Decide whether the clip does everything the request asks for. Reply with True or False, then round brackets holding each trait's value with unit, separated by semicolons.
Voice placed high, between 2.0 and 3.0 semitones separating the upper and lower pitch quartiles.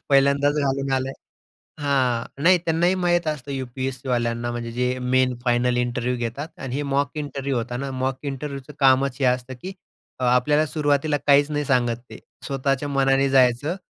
False (135 Hz; 2.4 semitones)